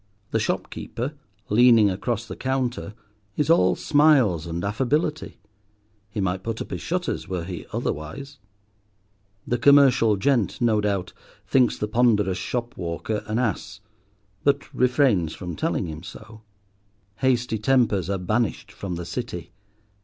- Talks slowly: Yes, slow, 130 wpm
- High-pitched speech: No, low, 110 Hz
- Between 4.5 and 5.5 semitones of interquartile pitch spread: Yes, average, 4.9 semitones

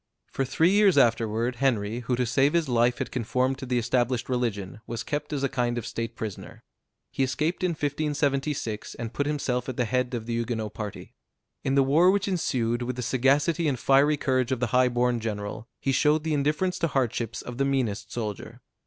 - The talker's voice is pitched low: Yes, low, 125 Hz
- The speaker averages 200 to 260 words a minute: Yes, fast, 205 wpm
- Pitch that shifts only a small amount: No, average, 3.4 semitones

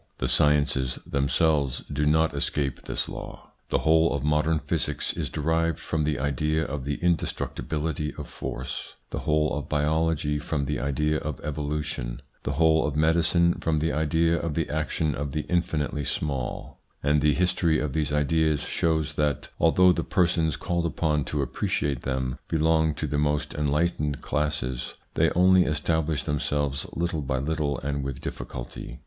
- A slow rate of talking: No, average, 160 wpm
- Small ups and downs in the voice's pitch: Yes, narrow, 2.0 semitones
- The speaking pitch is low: Yes, very low, 75 Hz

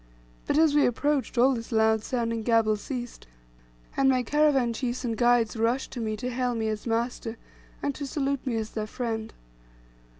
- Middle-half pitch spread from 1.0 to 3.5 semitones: Yes, average, 2.9 semitones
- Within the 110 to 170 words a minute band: No, average, 180 wpm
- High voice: Yes, high, 240 Hz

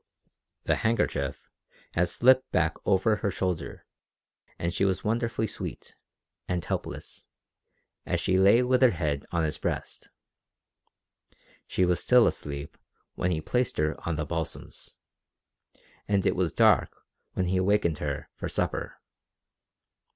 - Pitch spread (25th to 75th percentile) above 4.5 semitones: Yes, average, 5.2 semitones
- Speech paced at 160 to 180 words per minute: No, slow, 135 wpm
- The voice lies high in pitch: No, very low, 90 Hz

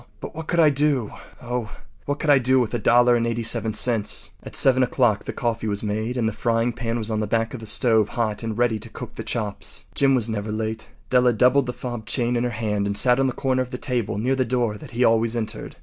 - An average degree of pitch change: No, narrow, 2.3 semitones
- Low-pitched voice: Yes, low, 120 Hz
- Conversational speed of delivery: No, fast, 260 wpm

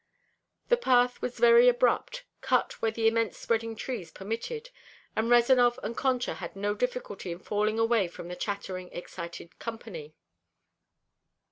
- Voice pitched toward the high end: Yes, high, 225 Hz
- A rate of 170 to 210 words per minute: No, average, 140 wpm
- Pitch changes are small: No, average, 3.9 semitones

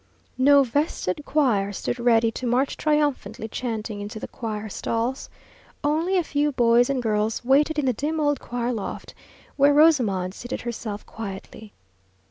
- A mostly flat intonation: No, average, 4.7 semitones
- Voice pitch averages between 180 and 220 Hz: No, high, 245 Hz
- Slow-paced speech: No, average, 150 wpm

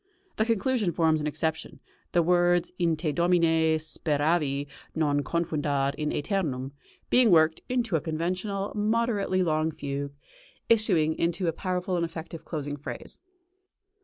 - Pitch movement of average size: Yes, average, 3.2 semitones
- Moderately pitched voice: Yes, medium, 165 Hz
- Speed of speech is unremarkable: No, slow, 130 wpm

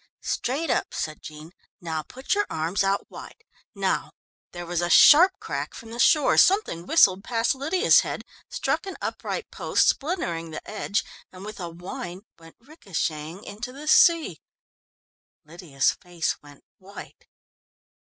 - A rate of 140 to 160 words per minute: Yes, average, 155 wpm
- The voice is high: Yes, high, 195 Hz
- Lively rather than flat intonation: Yes, wide, 8.9 semitones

